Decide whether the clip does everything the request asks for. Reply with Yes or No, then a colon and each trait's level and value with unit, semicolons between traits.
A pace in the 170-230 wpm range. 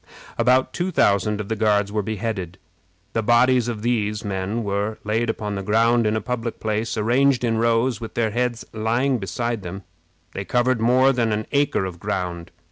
Yes: average, 190 wpm